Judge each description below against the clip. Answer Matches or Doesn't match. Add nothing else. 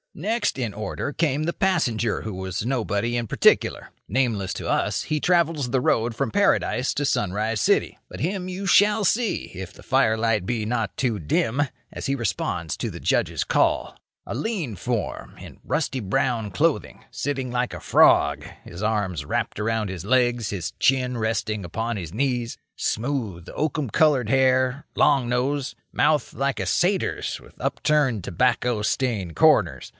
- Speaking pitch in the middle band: Doesn't match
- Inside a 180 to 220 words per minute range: Doesn't match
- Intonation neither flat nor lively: Matches